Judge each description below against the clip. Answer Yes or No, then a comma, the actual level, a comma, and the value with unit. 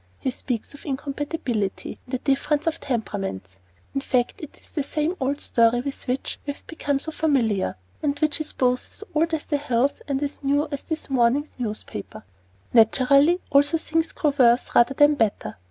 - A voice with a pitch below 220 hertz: No, very high, 275 Hz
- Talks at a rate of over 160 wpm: Yes, average, 185 wpm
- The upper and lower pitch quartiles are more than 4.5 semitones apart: No, average, 3.4 semitones